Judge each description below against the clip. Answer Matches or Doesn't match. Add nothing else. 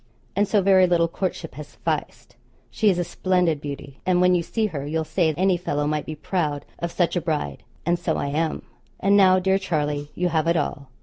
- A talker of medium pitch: Matches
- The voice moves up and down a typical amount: Matches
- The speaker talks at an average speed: Doesn't match